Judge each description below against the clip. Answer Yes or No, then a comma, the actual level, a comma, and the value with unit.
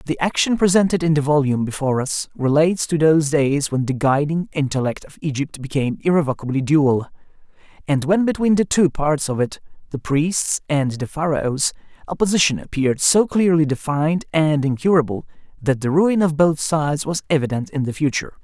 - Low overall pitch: No, medium, 150 Hz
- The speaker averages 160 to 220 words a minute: Yes, average, 170 wpm